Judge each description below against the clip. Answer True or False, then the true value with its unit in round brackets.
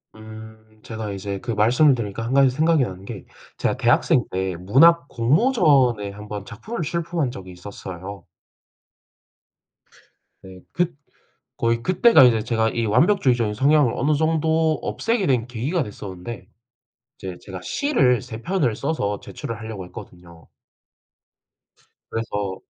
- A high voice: False (115 Hz)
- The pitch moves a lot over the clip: True (6.7 semitones)